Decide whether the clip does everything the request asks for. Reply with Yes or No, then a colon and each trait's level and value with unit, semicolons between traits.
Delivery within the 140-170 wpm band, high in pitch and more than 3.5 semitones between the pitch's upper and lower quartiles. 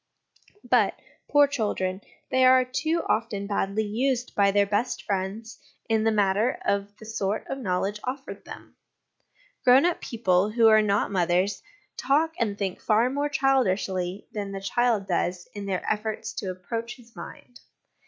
Yes: average, 155 wpm; high, 215 Hz; average, 3.9 semitones